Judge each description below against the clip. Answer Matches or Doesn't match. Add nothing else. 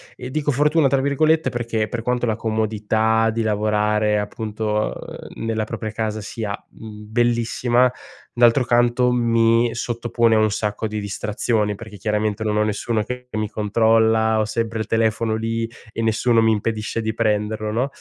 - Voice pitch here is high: Doesn't match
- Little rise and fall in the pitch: Matches